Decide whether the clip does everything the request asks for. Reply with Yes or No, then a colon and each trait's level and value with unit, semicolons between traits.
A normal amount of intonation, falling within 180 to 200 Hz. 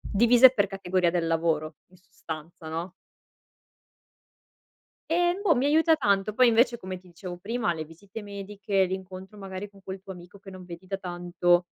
Yes: average, 3.0 semitones; high, 190 Hz